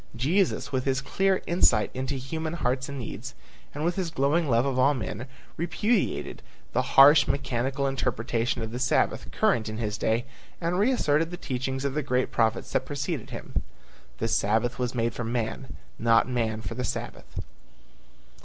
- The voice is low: Yes, low, 130 Hz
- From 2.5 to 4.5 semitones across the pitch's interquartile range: Yes, average, 3.9 semitones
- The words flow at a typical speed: Yes, average, 165 wpm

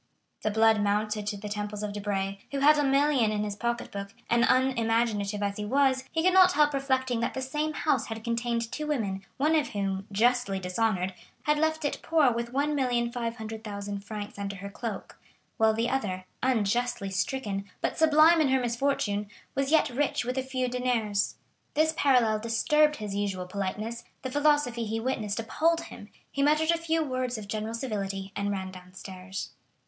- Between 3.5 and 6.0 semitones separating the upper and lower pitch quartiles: Yes, average, 4.9 semitones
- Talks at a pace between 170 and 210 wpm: Yes, average, 180 wpm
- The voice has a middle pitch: No, high, 230 Hz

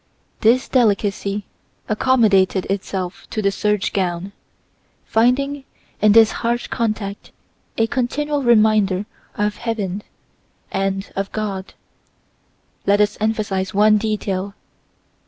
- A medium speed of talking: No, slow, 100 wpm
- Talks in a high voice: Yes, high, 210 Hz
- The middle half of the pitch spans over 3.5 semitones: No, narrow, 2.5 semitones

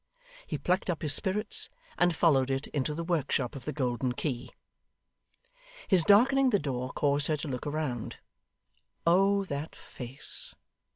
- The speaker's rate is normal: Yes, average, 150 wpm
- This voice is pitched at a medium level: Yes, medium, 150 Hz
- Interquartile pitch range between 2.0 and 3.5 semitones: No, average, 5.0 semitones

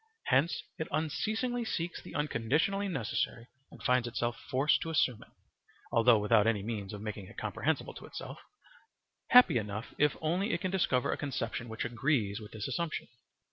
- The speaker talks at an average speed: Yes, average, 170 wpm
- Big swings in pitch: Yes, wide, 6.4 semitones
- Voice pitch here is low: Yes, low, 125 Hz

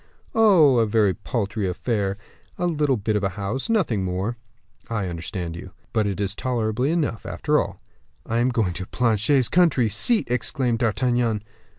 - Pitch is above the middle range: No, low, 115 Hz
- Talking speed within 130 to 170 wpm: Yes, average, 165 wpm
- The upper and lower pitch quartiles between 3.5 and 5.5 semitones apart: Yes, average, 4.4 semitones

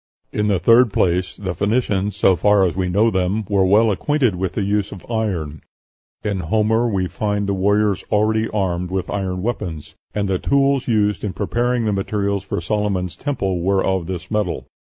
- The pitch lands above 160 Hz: No, low, 100 Hz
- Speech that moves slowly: No, average, 185 wpm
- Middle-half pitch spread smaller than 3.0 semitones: Yes, narrow, 2.5 semitones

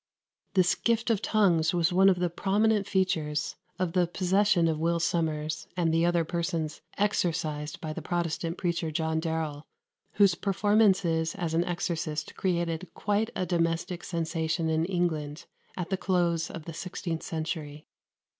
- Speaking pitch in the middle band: Yes, medium, 170 Hz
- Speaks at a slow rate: No, average, 150 wpm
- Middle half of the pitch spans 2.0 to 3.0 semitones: Yes, narrow, 2.5 semitones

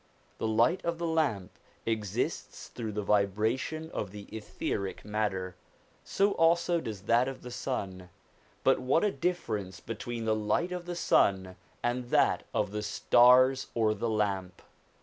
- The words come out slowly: No, average, 155 wpm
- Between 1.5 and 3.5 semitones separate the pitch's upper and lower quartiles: No, average, 4.7 semitones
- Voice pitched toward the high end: No, low, 110 Hz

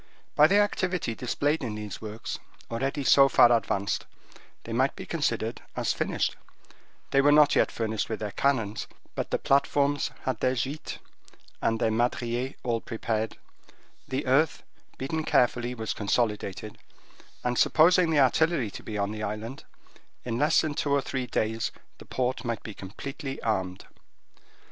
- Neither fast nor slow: Yes, average, 155 wpm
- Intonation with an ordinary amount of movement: Yes, average, 4.2 semitones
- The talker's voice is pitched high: No, low, 125 Hz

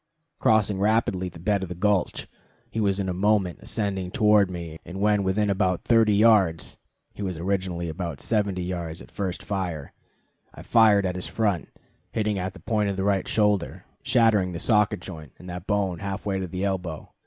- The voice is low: Yes, very low, 95 Hz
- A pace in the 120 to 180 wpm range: No, average, 195 wpm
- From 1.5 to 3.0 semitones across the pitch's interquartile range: Yes, narrow, 2.5 semitones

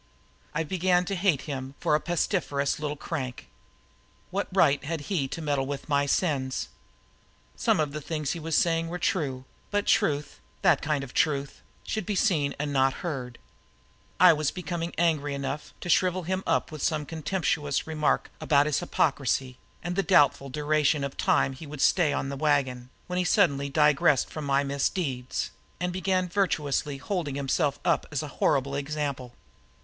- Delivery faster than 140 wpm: Yes, average, 170 wpm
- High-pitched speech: No, medium, 150 Hz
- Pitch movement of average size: Yes, average, 3.5 semitones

